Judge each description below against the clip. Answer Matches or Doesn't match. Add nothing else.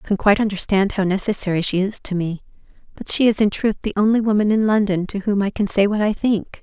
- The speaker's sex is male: Doesn't match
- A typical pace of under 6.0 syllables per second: Doesn't match